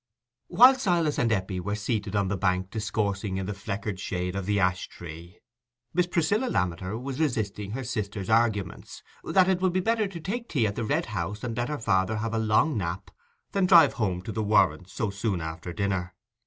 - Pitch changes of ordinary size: No, wide, 6.0 semitones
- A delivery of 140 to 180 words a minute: No, fast, 205 wpm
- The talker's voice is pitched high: No, low, 105 Hz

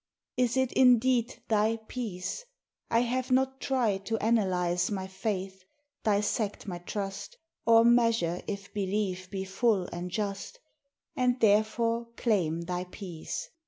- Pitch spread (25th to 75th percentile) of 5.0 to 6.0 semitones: No, average, 3.8 semitones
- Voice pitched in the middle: No, high, 210 Hz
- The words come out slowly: Yes, slow, 125 wpm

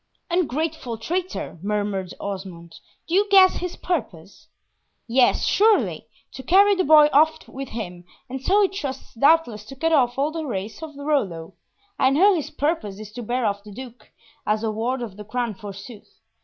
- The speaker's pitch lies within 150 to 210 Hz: No, very high, 250 Hz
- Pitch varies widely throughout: Yes, wide, 7.3 semitones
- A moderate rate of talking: Yes, average, 175 wpm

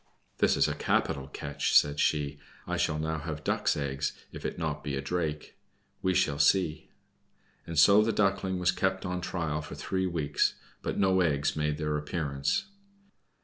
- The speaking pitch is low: Yes, very low, 80 Hz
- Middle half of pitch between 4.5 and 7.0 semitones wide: No, average, 3.7 semitones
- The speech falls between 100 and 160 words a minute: No, average, 175 wpm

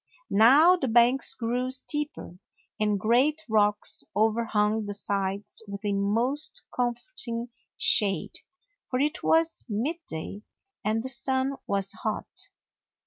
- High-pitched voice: Yes, high, 230 Hz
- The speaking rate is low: Yes, slow, 120 wpm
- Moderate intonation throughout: Yes, average, 4.3 semitones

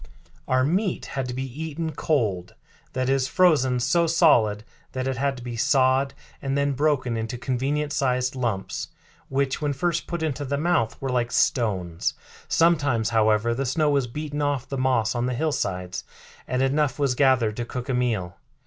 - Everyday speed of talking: Yes, average, 175 wpm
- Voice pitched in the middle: No, low, 130 Hz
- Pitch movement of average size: Yes, average, 3.4 semitones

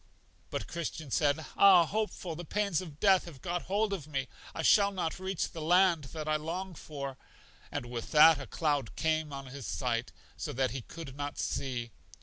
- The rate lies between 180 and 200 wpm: Yes, average, 190 wpm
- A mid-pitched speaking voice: Yes, medium, 155 Hz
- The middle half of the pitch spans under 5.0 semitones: Yes, average, 4.4 semitones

